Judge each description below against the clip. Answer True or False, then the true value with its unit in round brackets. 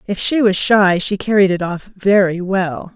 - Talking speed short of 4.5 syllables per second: True (4.3 syllables/s)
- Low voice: False (190 Hz)